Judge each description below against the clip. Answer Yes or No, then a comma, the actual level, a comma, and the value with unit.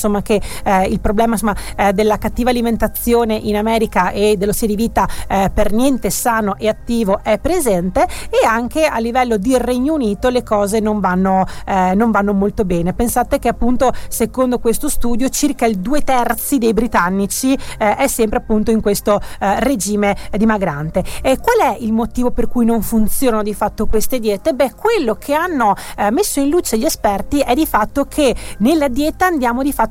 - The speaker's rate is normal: No, fast, 190 wpm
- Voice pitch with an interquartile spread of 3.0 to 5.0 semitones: Yes, average, 3.7 semitones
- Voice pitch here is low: No, high, 225 Hz